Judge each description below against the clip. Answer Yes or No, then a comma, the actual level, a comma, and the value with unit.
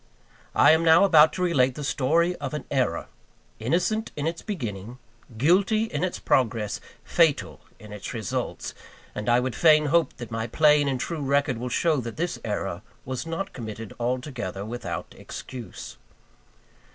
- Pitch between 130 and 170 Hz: Yes, low, 135 Hz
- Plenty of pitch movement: Yes, wide, 5.9 semitones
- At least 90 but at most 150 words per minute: No, average, 160 wpm